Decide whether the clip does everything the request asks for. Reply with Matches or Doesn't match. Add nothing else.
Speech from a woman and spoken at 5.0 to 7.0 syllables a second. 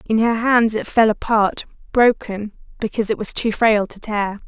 Doesn't match